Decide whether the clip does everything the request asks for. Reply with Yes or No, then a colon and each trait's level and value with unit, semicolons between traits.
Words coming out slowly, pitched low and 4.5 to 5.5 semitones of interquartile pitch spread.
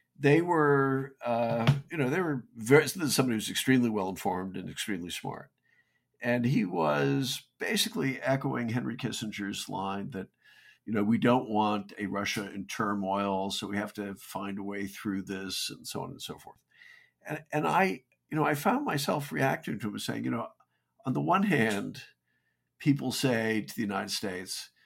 No: average, 175 wpm; low, 115 Hz; average, 5.0 semitones